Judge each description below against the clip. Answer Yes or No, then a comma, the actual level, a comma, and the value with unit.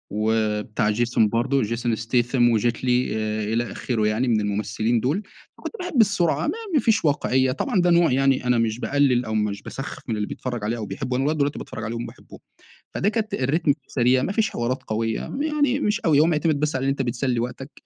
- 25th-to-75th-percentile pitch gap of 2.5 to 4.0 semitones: No, average, 4.7 semitones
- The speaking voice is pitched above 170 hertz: No, low, 125 Hz